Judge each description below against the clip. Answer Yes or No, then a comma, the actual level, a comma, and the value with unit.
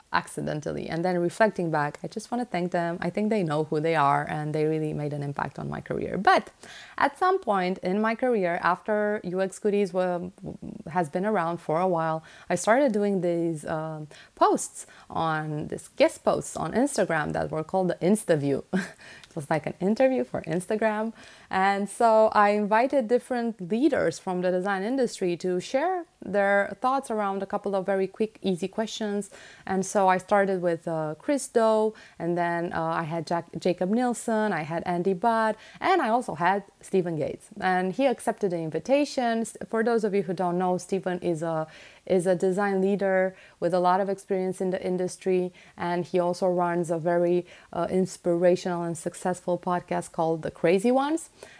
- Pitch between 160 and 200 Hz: Yes, medium, 185 Hz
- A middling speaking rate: Yes, average, 185 wpm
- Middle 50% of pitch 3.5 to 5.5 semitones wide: Yes, average, 3.8 semitones